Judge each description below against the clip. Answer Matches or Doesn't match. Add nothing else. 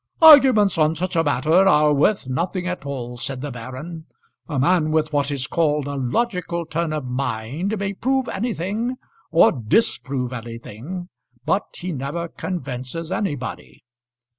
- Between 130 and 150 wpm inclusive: Matches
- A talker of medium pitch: Matches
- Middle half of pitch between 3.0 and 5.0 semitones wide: Doesn't match